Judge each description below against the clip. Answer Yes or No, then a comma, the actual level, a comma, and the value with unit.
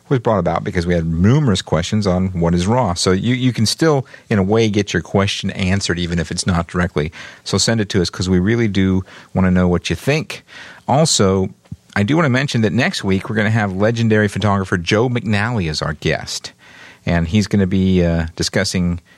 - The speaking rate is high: Yes, fast, 220 wpm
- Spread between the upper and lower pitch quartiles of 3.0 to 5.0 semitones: Yes, average, 3.7 semitones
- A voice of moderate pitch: No, very low, 95 Hz